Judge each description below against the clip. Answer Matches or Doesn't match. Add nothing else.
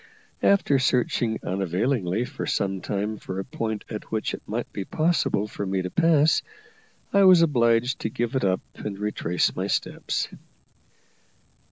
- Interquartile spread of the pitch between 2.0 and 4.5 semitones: Doesn't match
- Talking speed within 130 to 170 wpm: Matches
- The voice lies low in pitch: Matches